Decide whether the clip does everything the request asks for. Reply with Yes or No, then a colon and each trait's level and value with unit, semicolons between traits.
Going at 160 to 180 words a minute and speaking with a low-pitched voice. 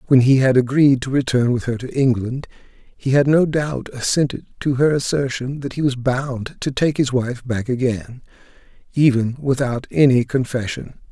Yes: average, 175 wpm; low, 130 Hz